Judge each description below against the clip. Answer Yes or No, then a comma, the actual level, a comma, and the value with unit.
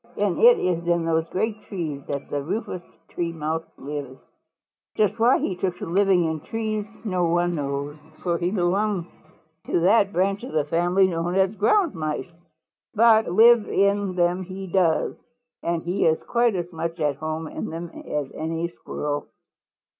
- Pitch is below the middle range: No, medium, 175 Hz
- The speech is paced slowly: No, average, 170 wpm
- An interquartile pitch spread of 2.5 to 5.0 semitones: Yes, average, 3.5 semitones